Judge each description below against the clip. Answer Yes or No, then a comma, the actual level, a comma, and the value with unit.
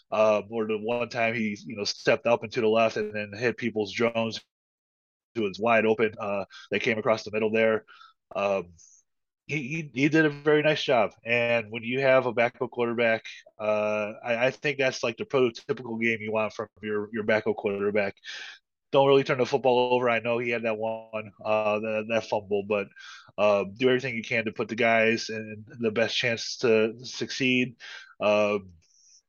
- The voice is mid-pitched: No, low, 115 Hz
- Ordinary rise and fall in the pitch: No, narrow, 2.1 semitones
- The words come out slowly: No, average, 195 wpm